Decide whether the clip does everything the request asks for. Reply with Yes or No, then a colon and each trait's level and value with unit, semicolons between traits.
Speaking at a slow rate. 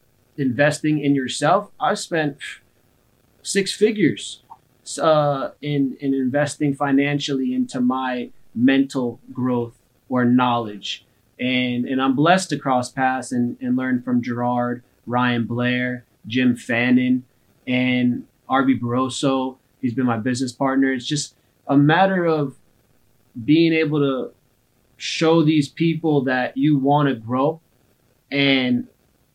Yes: slow, 120 wpm